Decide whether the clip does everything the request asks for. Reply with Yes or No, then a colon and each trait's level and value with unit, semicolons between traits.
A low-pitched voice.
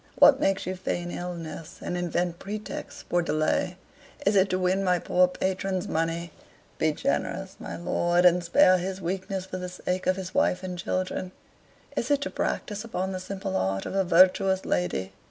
No: medium, 185 Hz